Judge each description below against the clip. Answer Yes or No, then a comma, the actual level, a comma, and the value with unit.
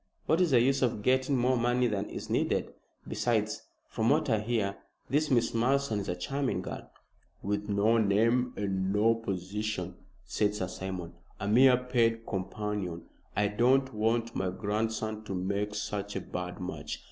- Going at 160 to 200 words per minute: Yes, average, 165 wpm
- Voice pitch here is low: Yes, low, 110 Hz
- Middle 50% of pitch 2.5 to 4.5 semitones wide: Yes, average, 3.5 semitones